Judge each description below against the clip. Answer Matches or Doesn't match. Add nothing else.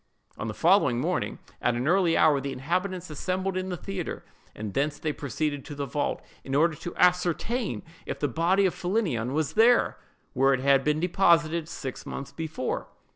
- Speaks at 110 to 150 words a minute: Doesn't match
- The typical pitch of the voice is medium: Matches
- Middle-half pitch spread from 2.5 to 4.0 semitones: Doesn't match